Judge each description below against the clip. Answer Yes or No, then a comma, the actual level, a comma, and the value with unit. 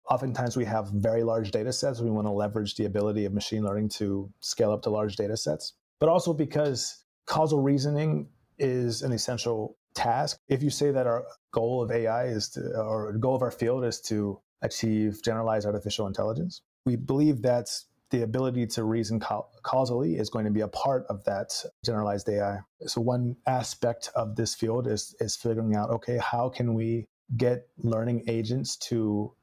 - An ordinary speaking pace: Yes, average, 185 wpm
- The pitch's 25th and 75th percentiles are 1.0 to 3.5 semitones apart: Yes, average, 2.8 semitones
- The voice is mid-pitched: No, low, 115 Hz